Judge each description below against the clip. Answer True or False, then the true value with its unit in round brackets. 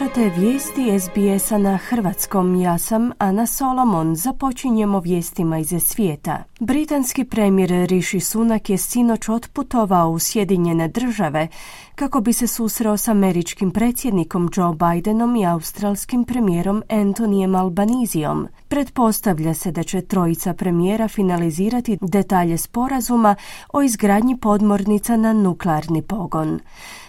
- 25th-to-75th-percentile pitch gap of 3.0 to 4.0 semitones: False (4.4 semitones)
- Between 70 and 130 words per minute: True (115 wpm)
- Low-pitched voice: False (205 Hz)